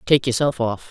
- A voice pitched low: Yes, low, 125 Hz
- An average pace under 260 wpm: Yes, average, 200 wpm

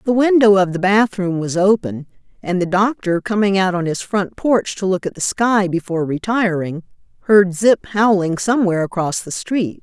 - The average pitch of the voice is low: No, high, 190 Hz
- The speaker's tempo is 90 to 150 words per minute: No, average, 185 wpm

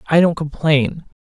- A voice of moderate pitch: Yes, medium, 150 Hz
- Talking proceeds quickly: No, average, 145 wpm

